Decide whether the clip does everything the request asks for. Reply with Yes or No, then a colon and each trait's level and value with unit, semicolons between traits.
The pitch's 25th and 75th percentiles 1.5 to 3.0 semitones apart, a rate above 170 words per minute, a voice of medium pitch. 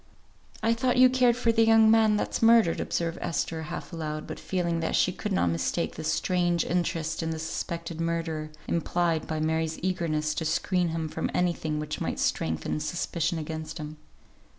Yes: narrow, 2.6 semitones; average, 180 wpm; medium, 165 Hz